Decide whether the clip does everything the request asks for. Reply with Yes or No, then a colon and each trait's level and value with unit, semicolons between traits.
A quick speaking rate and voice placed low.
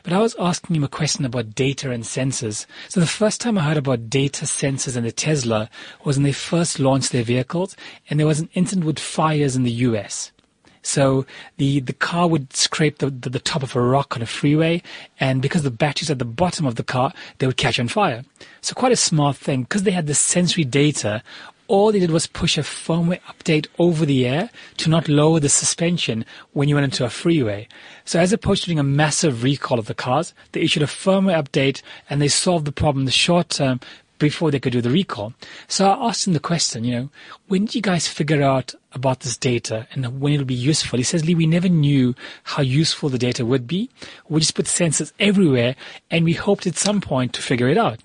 No: fast, 230 wpm; medium, 150 Hz